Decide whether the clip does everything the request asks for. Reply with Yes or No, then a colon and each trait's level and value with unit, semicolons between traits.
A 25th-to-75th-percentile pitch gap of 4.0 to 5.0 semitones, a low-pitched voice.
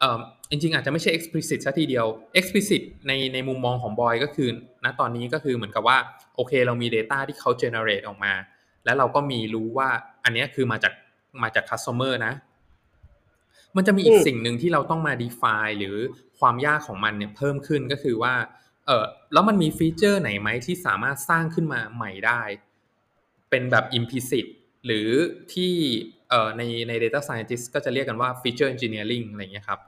Yes: average, 4.4 semitones; low, 130 Hz